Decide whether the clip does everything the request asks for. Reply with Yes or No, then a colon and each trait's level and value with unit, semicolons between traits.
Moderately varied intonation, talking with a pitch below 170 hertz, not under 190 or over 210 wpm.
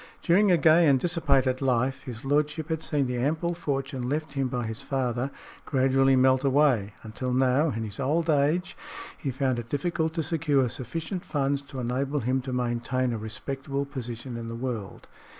No: average, 3.1 semitones; low, 135 Hz; average, 180 wpm